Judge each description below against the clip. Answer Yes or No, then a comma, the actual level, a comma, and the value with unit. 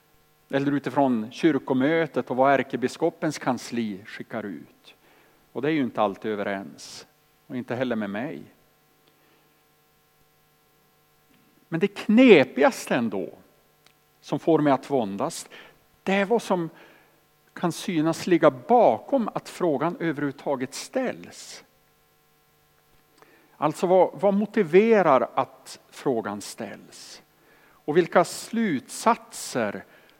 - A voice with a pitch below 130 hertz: No, low, 135 Hz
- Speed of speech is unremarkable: No, slow, 105 wpm